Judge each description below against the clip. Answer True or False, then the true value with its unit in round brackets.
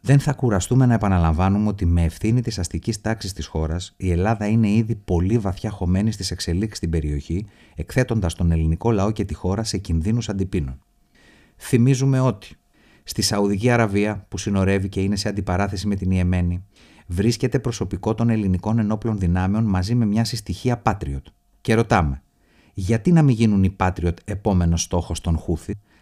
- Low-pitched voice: True (100 Hz)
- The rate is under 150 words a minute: False (165 wpm)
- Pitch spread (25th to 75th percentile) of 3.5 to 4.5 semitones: True (4.2 semitones)